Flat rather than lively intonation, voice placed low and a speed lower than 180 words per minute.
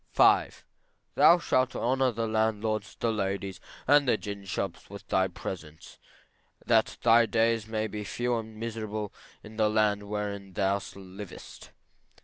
Yes: narrow, 2.2 semitones; low, 110 Hz; average, 140 wpm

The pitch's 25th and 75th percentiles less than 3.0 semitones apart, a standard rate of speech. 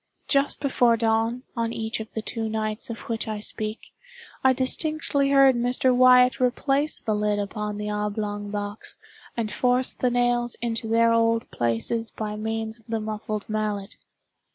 Yes: narrow, 2.6 semitones; average, 160 wpm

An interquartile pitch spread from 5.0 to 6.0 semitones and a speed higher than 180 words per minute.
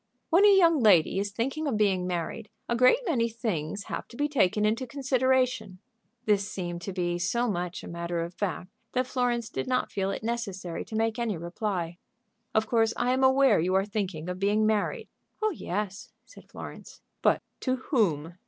Yes: wide, 5.6 semitones; average, 190 wpm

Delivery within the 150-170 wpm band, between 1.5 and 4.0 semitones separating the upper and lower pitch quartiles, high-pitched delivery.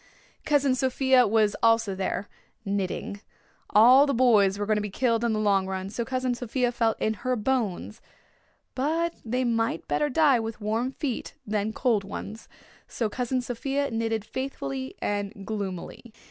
Yes: average, 160 wpm; average, 3.7 semitones; high, 225 Hz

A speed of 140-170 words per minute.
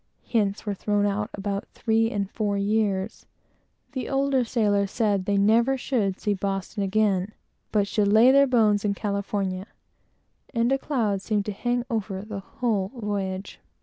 Yes: average, 160 wpm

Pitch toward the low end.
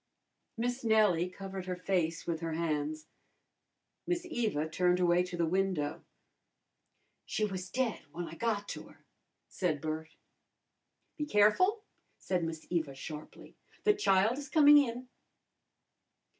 No: medium, 185 Hz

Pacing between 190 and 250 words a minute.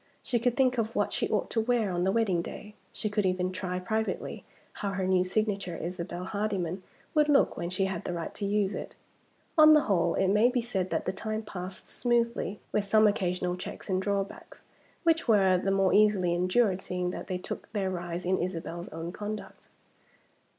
Yes: average, 200 wpm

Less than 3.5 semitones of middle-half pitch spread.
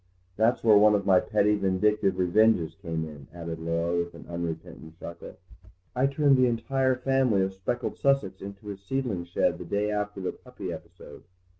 No: average, 4.6 semitones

